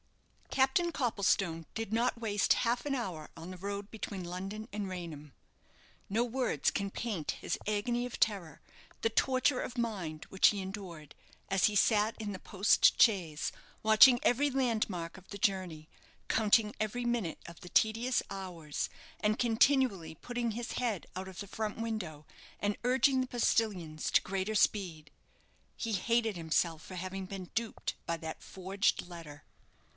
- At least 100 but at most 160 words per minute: Yes, average, 155 wpm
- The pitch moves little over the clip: No, average, 4.5 semitones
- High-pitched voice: Yes, high, 205 Hz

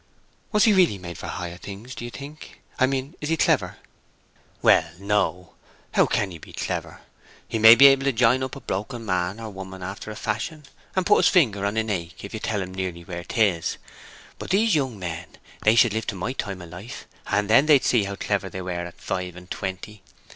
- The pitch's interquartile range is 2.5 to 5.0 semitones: No, wide, 5.5 semitones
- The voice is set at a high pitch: No, low, 105 Hz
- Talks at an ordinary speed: No, fast, 220 wpm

